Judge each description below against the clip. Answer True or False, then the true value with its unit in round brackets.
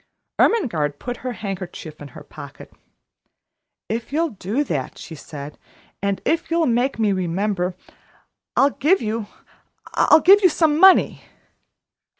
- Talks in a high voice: True (220 Hz)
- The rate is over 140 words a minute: False (135 wpm)